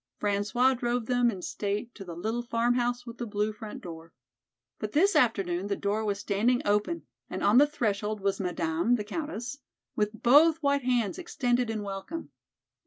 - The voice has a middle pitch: No, high, 220 Hz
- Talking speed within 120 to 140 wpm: No, average, 175 wpm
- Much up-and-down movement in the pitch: No, average, 3.4 semitones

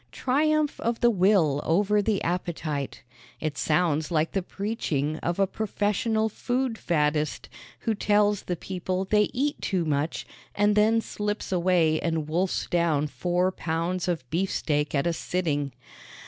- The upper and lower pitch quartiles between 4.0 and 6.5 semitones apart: Yes, average, 4.8 semitones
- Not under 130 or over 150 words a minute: Yes, average, 145 wpm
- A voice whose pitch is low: No, medium, 180 Hz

